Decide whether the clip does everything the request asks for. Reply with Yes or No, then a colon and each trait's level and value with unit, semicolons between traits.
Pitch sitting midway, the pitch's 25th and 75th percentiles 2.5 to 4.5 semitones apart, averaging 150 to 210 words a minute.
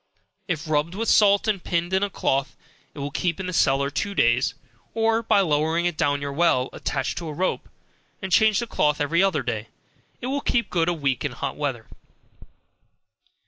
No: medium, 170 Hz; wide, 5.6 semitones; average, 195 wpm